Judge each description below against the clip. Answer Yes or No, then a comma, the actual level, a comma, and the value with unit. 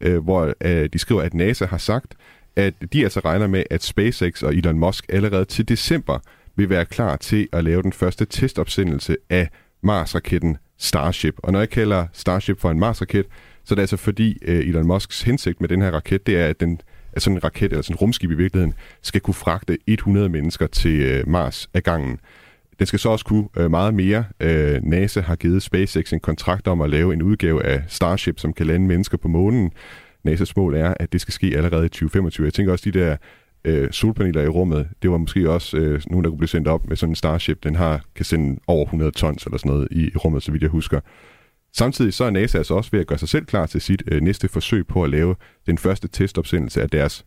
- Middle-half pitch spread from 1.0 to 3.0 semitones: No, average, 3.5 semitones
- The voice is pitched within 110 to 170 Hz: No, very low, 90 Hz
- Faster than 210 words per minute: Yes, average, 220 wpm